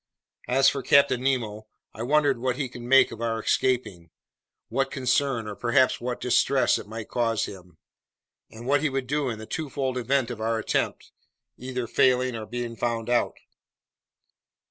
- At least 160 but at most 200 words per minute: Yes, average, 165 wpm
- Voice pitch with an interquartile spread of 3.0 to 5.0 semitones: No, narrow, 2.6 semitones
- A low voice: Yes, low, 125 Hz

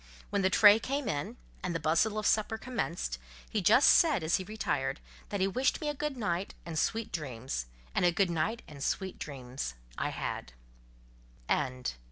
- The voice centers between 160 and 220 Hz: Yes, high, 190 Hz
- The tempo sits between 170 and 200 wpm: Yes, average, 180 wpm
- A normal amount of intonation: No, wide, 6.1 semitones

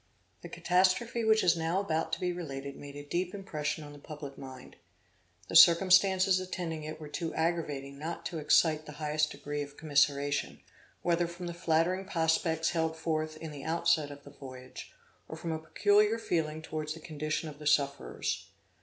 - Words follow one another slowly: No, average, 180 wpm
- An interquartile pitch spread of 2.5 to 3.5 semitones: Yes, average, 2.8 semitones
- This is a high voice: No, medium, 160 Hz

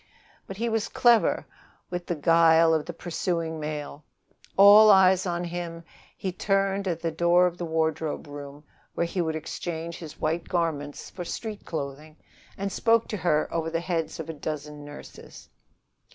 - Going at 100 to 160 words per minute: No, average, 170 wpm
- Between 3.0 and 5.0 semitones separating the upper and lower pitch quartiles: No, narrow, 2.6 semitones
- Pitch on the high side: No, medium, 170 Hz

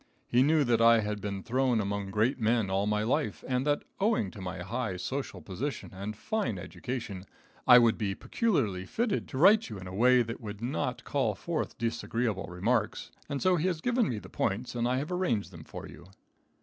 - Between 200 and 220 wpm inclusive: Yes, fast, 205 wpm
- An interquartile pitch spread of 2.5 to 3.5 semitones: No, average, 4.8 semitones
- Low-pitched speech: Yes, low, 115 Hz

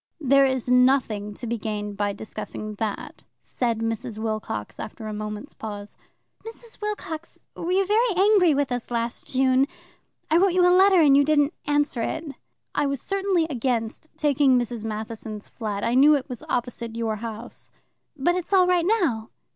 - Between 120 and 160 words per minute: No, average, 170 wpm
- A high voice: Yes, very high, 250 Hz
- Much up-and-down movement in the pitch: Yes, wide, 6.3 semitones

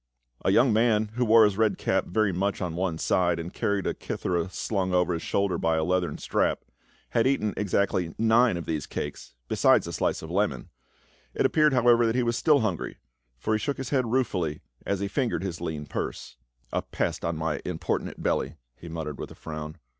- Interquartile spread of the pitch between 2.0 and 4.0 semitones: No, average, 5.2 semitones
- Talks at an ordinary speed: No, fast, 215 wpm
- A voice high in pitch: No, very low, 95 Hz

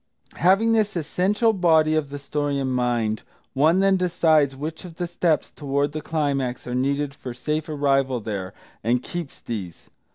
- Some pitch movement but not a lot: Yes, average, 4.2 semitones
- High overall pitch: No, medium, 145 Hz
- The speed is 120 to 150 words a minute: No, average, 165 wpm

